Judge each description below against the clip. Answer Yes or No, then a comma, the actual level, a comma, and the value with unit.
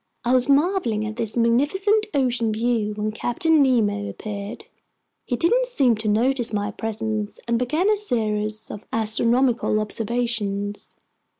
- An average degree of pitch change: Yes, average, 3.6 semitones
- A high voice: Yes, high, 230 Hz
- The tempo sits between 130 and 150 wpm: Yes, slow, 135 wpm